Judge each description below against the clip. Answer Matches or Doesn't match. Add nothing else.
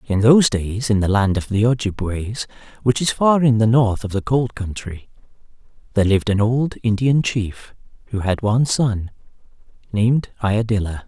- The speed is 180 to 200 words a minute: Doesn't match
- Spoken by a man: Matches